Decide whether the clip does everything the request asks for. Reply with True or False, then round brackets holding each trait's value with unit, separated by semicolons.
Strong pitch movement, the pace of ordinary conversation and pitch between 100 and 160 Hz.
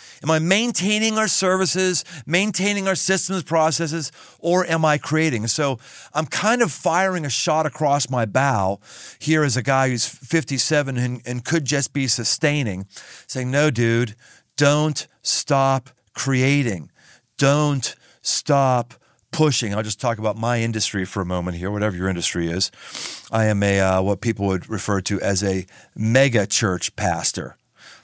True (6.3 semitones; 155 wpm; 135 Hz)